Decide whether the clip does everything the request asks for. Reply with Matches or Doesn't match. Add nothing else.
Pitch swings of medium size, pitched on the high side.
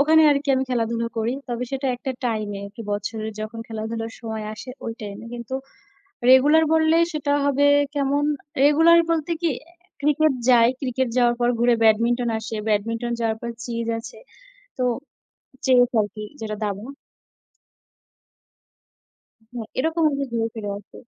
Matches